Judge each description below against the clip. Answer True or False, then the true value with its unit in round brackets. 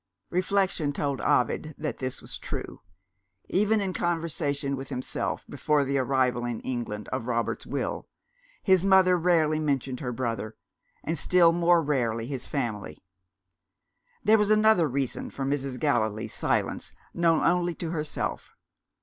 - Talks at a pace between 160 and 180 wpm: False (140 wpm)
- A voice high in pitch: False (145 Hz)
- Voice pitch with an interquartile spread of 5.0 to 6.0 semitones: True (5.4 semitones)